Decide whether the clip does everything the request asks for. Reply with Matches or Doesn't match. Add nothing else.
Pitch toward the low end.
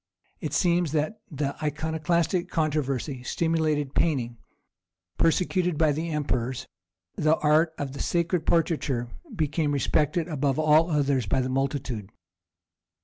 Doesn't match